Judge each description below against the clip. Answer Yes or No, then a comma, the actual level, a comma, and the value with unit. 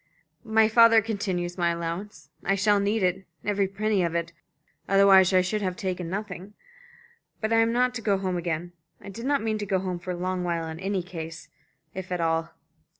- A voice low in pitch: No, high, 190 Hz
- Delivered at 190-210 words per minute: Yes, fast, 205 wpm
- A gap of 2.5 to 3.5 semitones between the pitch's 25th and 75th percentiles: Yes, average, 3.0 semitones